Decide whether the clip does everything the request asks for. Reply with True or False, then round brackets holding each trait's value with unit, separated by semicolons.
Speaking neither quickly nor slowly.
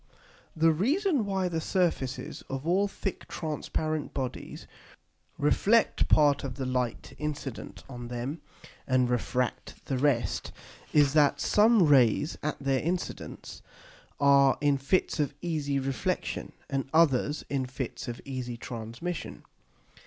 False (125 wpm)